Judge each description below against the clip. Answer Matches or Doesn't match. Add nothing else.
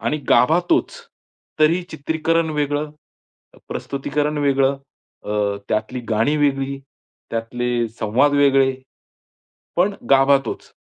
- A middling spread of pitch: Matches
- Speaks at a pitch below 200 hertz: Matches